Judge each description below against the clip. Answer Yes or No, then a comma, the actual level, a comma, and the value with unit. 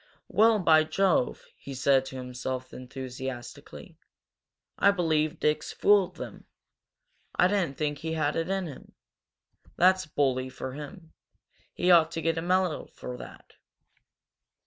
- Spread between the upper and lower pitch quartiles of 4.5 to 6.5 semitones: Yes, average, 5.2 semitones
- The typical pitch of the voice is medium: Yes, medium, 155 Hz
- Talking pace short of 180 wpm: Yes, slow, 135 wpm